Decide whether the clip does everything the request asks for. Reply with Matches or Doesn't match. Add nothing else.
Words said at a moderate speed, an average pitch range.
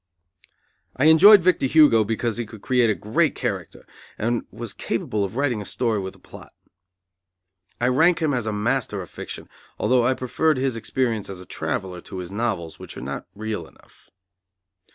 Matches